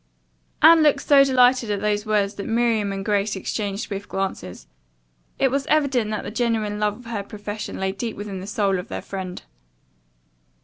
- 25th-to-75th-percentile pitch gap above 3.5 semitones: No, average, 3.2 semitones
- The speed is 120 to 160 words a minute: No, average, 180 wpm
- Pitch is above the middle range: Yes, high, 210 Hz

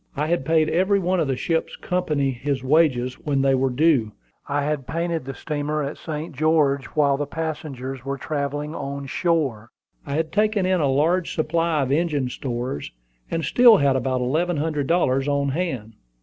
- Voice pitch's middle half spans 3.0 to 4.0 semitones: Yes, average, 3.4 semitones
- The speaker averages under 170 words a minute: No, average, 180 wpm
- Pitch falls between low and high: Yes, medium, 145 Hz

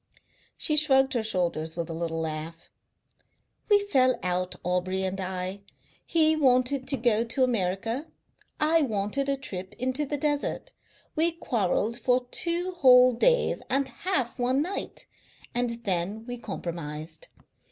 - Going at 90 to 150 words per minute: Yes, average, 140 wpm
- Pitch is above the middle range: Yes, high, 240 Hz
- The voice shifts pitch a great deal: Yes, wide, 7.0 semitones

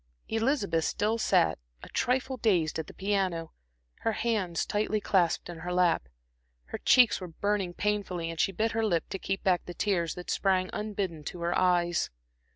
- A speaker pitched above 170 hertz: Yes, high, 190 Hz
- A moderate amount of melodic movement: Yes, average, 3.4 semitones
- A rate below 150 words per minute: No, average, 175 wpm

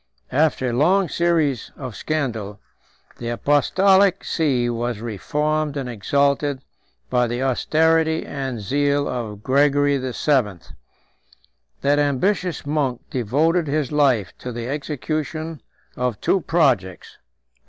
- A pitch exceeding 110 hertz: Yes, medium, 140 Hz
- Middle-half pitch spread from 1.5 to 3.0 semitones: No, average, 4.1 semitones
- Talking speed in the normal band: No, slow, 110 wpm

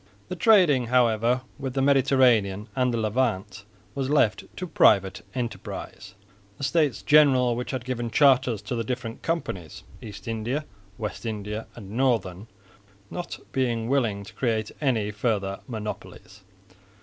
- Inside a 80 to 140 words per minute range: Yes, slow, 135 wpm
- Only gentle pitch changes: No, average, 3.7 semitones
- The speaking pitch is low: Yes, low, 120 Hz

